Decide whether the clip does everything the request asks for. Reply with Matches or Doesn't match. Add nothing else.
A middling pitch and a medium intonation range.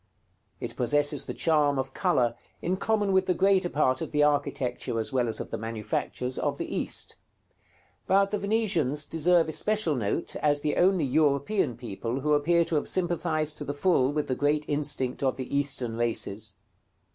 Matches